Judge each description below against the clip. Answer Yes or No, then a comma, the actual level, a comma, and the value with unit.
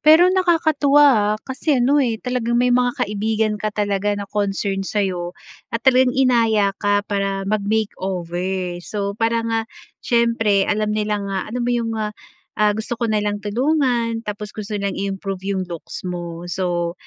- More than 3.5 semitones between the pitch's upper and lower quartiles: No, average, 3.2 semitones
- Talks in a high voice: Yes, high, 210 Hz